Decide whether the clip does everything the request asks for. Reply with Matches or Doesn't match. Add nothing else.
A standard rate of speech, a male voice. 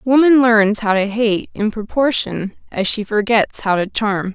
Doesn't match